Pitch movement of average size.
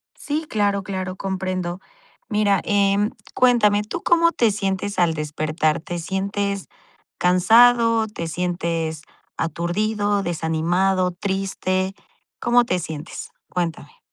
Yes: average, 3.1 semitones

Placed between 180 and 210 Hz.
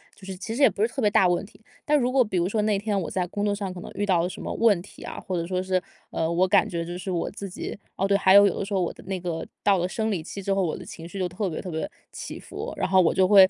Yes: high, 190 Hz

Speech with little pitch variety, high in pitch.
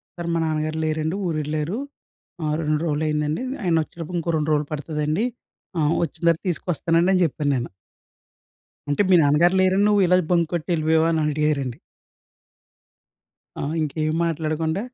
No: narrow, 1.9 semitones; medium, 155 Hz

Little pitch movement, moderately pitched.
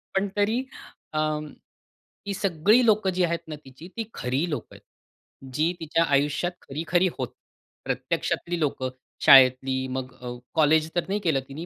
No: average, 4.8 semitones; medium, 160 Hz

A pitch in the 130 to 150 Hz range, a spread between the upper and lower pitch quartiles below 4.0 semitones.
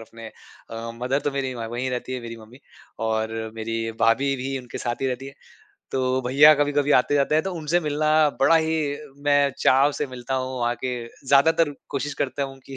Yes: low, 135 Hz; average, 2.9 semitones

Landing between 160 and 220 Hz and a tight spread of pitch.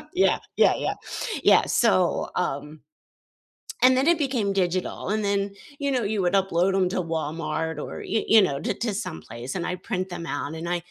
No: medium, 185 Hz; average, 5.2 semitones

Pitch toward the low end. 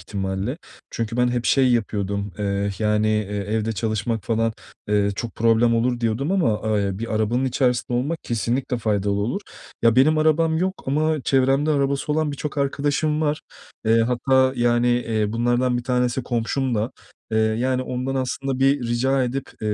Yes: low, 120 Hz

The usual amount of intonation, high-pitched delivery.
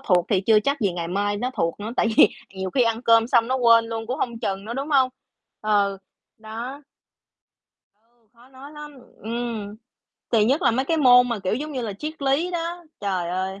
Yes: average, 4.5 semitones; high, 230 Hz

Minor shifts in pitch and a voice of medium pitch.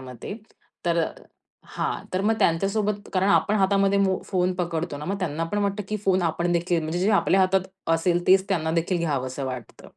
No: average, 3.0 semitones; medium, 180 Hz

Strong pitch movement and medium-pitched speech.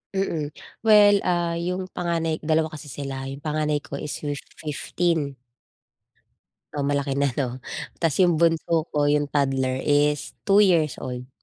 No: average, 3.1 semitones; medium, 150 Hz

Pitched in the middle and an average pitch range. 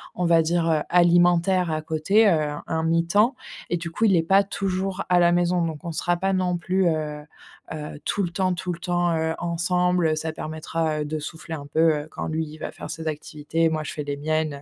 No: medium, 165 Hz; narrow, 2.2 semitones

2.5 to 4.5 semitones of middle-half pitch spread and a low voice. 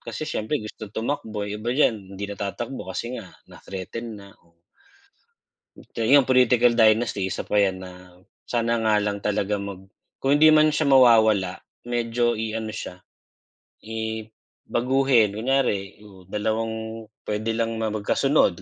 Yes: average, 2.8 semitones; low, 110 Hz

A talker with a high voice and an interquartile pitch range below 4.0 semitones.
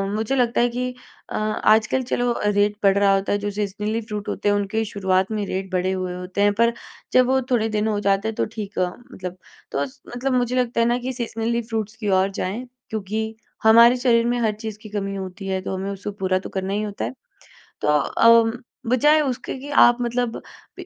Yes: high, 215 Hz; average, 3.2 semitones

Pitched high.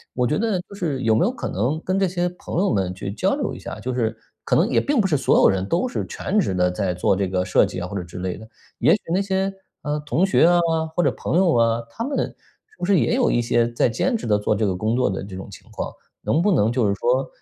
No: low, 125 Hz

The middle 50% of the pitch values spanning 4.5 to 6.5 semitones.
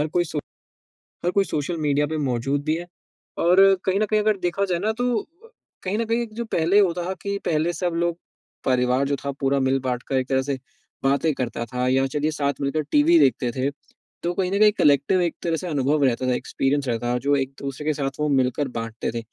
Yes: average, 5.1 semitones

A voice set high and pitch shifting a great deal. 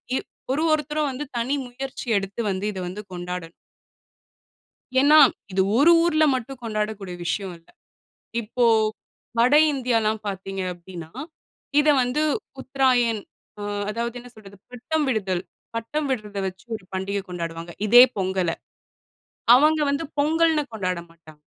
Yes: high, 220 Hz; wide, 6.2 semitones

